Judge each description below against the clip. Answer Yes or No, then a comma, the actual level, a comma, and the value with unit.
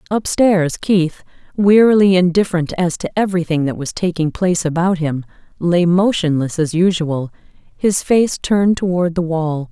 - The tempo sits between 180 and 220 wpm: No, average, 140 wpm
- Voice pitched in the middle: Yes, medium, 175 Hz